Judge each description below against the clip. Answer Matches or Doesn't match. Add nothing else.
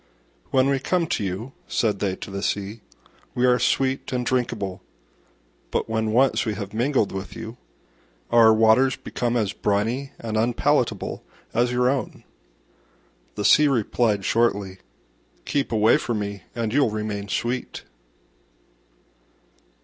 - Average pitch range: Matches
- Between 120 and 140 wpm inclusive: Matches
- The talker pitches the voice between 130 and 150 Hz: Doesn't match